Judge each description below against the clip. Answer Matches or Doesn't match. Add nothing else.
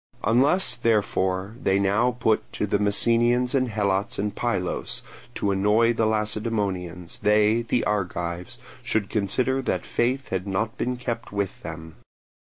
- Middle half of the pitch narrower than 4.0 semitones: Matches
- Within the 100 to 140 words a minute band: Matches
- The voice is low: Matches